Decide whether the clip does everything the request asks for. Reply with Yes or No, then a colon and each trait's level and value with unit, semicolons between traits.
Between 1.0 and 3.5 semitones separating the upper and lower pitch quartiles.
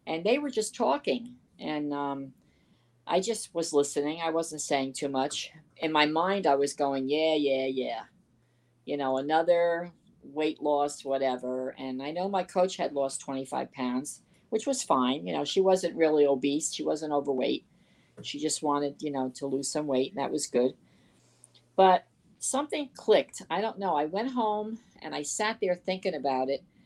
No: average, 5.2 semitones